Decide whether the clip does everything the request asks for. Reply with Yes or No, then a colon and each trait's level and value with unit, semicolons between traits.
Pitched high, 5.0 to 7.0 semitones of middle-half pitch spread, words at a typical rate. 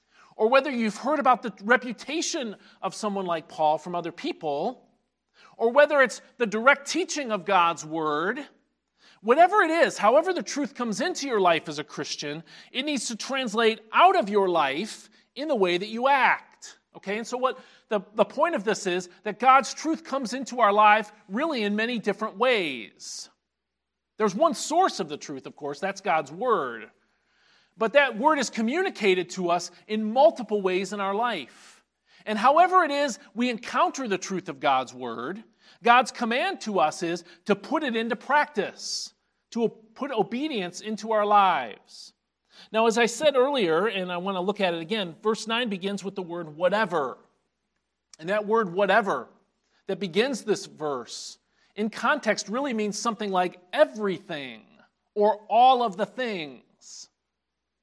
Yes: high, 220 Hz; wide, 5.4 semitones; average, 170 wpm